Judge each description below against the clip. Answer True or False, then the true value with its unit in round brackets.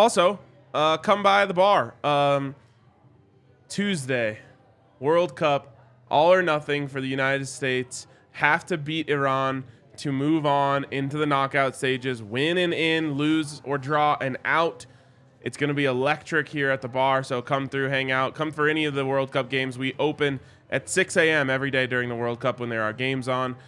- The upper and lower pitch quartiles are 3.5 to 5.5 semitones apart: False (2.6 semitones)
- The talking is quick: False (190 wpm)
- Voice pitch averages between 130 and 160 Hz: True (135 Hz)